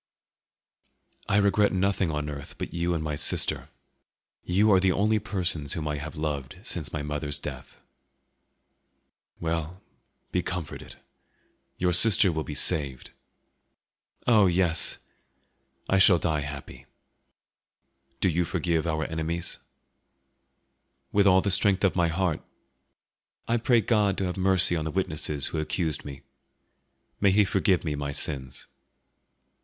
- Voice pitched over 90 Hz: No, very low, 85 Hz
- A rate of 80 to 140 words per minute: Yes, slow, 135 wpm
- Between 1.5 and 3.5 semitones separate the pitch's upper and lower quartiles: No, average, 4.0 semitones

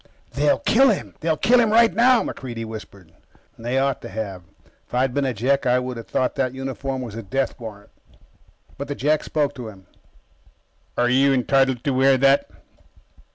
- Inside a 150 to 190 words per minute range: Yes, average, 185 wpm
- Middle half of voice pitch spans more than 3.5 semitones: No, average, 2.8 semitones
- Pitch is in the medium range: No, low, 130 Hz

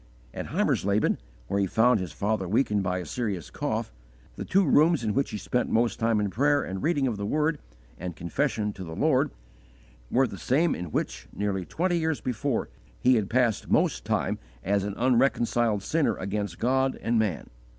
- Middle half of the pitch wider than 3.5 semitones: Yes, average, 5.2 semitones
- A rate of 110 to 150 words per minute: No, average, 185 wpm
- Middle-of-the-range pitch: No, low, 110 Hz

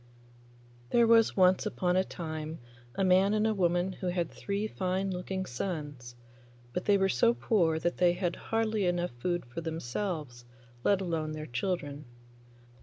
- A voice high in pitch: No, medium, 180 Hz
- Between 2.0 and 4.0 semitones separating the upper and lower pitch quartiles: Yes, average, 3.5 semitones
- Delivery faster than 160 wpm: No, average, 155 wpm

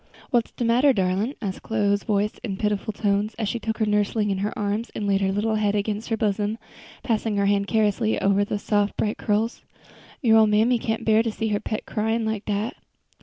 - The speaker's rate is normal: No, fast, 215 wpm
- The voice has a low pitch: No, high, 210 Hz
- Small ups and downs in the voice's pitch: Yes, narrow, 1.6 semitones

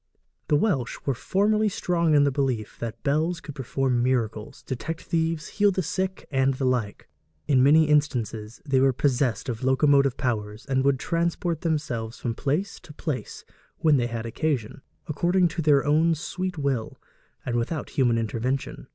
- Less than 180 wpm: Yes, average, 165 wpm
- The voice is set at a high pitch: No, medium, 140 Hz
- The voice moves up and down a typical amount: Yes, average, 4.7 semitones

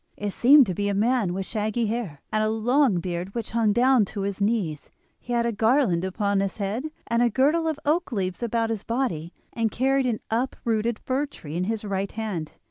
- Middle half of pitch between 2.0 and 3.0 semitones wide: No, average, 3.7 semitones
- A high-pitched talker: Yes, high, 220 Hz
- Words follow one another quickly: Yes, fast, 210 wpm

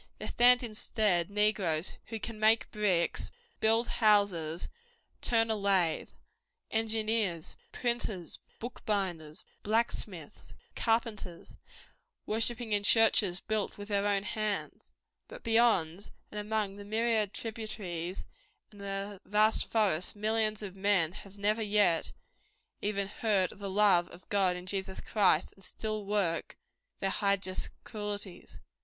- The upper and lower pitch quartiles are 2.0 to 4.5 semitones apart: Yes, narrow, 2.5 semitones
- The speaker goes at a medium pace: No, slow, 125 wpm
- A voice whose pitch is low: No, high, 205 Hz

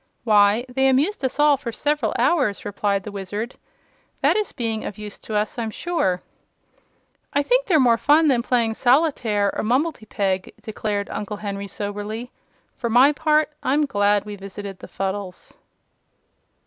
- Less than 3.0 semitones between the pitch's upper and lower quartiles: No, average, 5.3 semitones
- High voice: Yes, high, 225 Hz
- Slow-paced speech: No, average, 155 wpm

